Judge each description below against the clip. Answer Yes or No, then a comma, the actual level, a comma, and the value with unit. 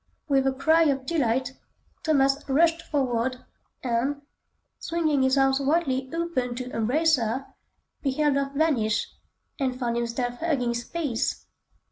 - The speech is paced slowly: Yes, slow, 125 wpm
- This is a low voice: No, very high, 270 Hz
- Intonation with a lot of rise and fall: No, average, 3.6 semitones